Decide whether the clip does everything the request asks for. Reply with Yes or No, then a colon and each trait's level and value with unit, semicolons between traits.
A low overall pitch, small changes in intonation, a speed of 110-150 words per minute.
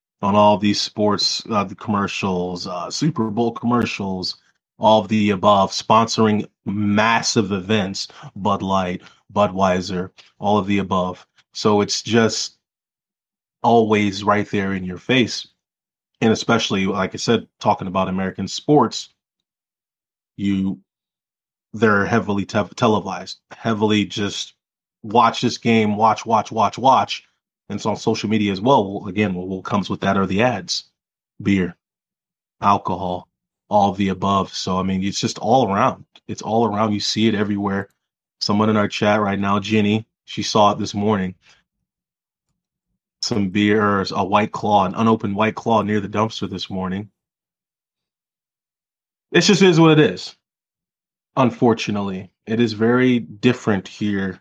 Yes: low, 105 Hz; narrow, 2.3 semitones; average, 140 wpm